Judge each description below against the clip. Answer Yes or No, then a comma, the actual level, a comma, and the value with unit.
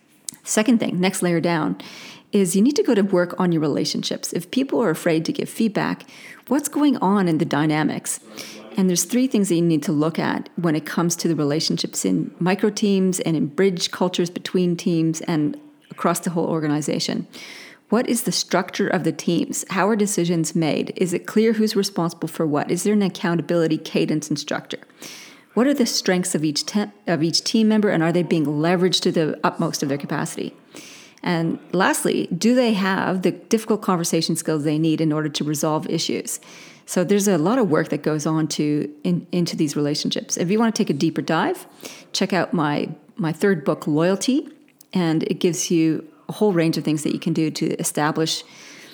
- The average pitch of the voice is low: No, medium, 180 Hz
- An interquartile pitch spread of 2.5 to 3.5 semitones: No, average, 4.3 semitones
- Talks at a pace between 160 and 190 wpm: No, average, 200 wpm